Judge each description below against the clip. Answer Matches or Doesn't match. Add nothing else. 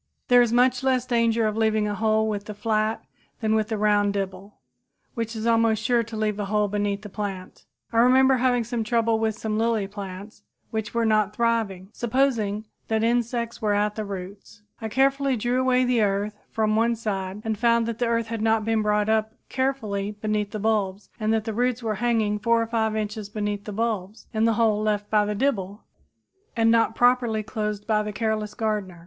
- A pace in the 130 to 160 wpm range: Doesn't match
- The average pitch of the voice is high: Matches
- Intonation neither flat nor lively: Doesn't match